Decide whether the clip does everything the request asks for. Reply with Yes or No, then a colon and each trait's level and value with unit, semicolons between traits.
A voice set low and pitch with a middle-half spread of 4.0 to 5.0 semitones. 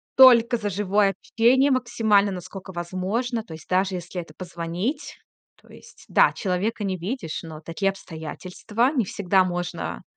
No: high, 195 Hz; average, 4.4 semitones